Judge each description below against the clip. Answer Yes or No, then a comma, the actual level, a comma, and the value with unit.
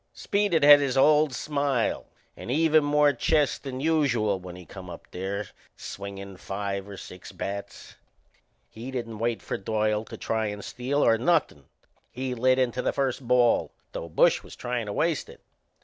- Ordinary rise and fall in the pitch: No, wide, 6.0 semitones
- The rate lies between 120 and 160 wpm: No, average, 170 wpm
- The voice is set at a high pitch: No, low, 120 Hz